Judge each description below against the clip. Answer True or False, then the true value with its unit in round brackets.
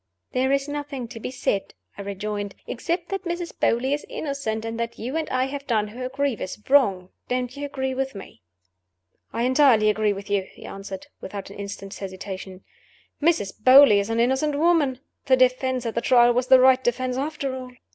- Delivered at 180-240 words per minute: True (195 wpm)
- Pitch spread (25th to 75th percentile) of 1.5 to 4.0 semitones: False (4.7 semitones)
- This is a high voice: True (255 Hz)